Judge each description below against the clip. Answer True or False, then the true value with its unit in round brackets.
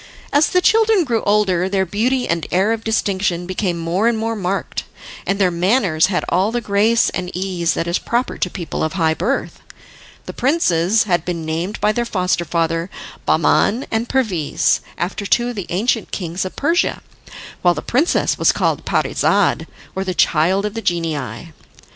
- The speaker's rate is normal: True (180 wpm)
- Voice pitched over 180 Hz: True (190 Hz)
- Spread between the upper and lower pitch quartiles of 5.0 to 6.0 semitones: False (4.6 semitones)